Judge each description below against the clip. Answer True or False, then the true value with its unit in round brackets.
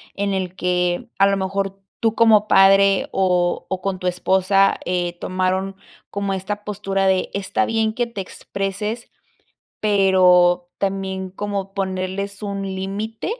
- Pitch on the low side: False (195 Hz)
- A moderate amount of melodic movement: False (1.3 semitones)